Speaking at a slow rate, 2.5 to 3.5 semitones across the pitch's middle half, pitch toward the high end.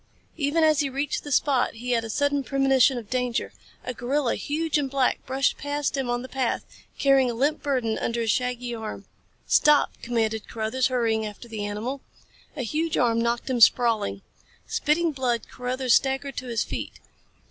No: average, 180 wpm; average, 3.0 semitones; very high, 255 Hz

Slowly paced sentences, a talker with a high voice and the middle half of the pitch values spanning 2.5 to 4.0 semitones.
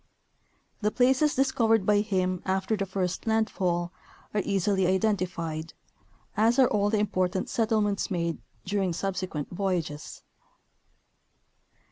Yes: slow, 110 wpm; high, 195 Hz; average, 2.9 semitones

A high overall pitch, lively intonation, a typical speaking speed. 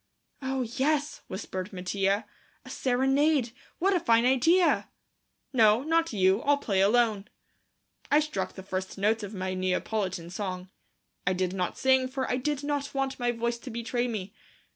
Yes: high, 235 Hz; wide, 5.7 semitones; average, 160 wpm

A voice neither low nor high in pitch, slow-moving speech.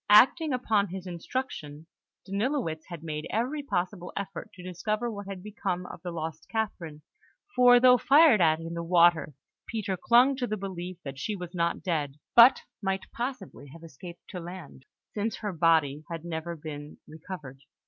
No: medium, 180 Hz; average, 170 wpm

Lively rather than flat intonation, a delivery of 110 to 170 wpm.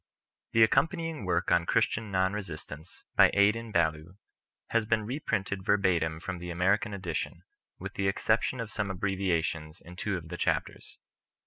No: average, 3.9 semitones; average, 155 wpm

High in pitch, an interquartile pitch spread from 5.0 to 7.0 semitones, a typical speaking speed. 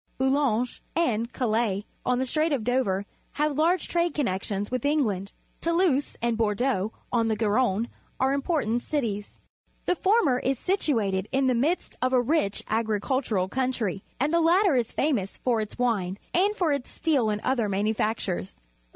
Yes: very high, 250 Hz; wide, 5.4 semitones; average, 160 wpm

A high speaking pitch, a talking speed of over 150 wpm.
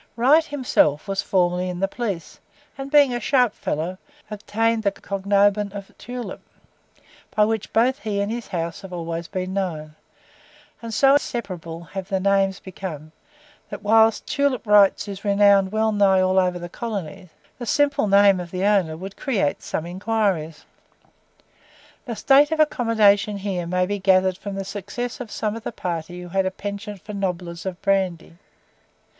Yes: high, 200 Hz; average, 165 wpm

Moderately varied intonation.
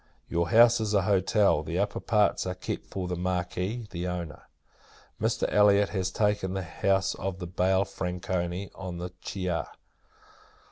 No: narrow, 2.2 semitones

